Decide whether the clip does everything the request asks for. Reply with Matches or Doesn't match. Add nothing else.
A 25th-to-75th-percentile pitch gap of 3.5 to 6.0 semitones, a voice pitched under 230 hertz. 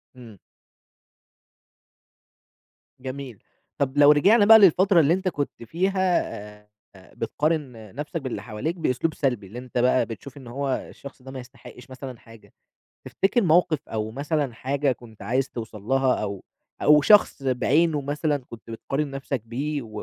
Matches